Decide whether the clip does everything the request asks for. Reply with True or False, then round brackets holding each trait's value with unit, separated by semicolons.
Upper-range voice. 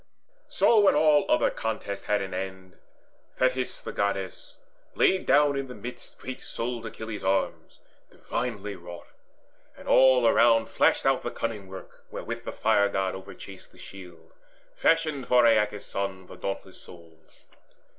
False (105 Hz)